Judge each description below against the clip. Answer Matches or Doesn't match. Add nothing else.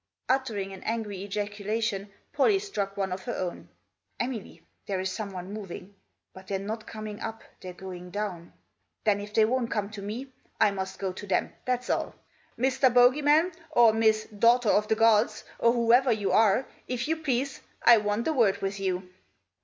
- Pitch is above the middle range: Matches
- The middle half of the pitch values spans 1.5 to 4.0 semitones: Matches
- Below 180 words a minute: Doesn't match